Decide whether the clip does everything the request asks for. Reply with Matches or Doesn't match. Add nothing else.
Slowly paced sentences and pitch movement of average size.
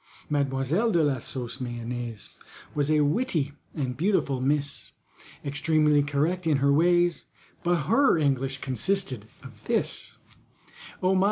Matches